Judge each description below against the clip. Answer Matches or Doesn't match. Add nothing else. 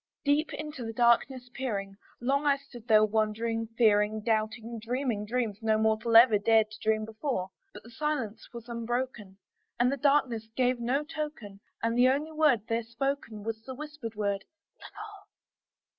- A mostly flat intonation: Doesn't match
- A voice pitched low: Doesn't match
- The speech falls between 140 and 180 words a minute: Matches